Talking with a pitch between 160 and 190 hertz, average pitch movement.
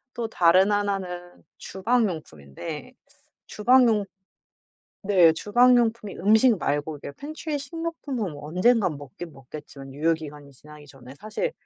No: medium, 185 Hz; wide, 7.6 semitones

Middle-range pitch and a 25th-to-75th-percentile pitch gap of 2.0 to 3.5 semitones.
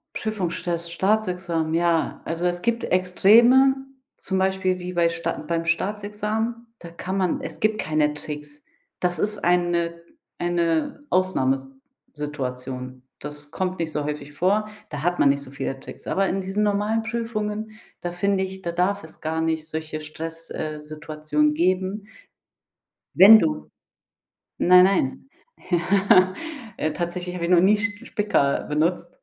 No: medium, 175 Hz; average, 4.0 semitones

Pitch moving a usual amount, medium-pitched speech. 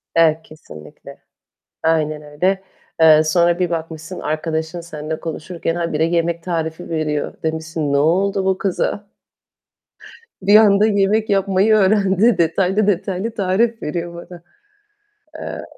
Yes: average, 3.4 semitones; medium, 170 Hz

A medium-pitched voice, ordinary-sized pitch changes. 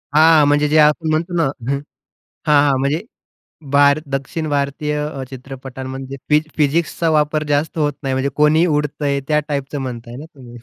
No: medium, 145 Hz; narrow, 1.9 semitones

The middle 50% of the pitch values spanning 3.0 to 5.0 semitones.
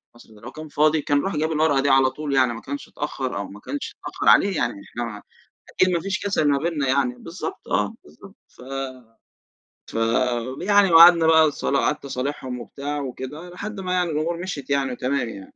Yes: average, 4.5 semitones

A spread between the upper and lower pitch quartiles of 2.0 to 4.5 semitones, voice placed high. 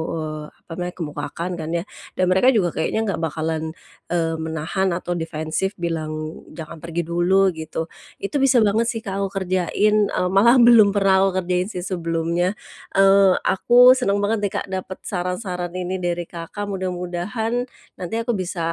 No: average, 2.9 semitones; medium, 180 Hz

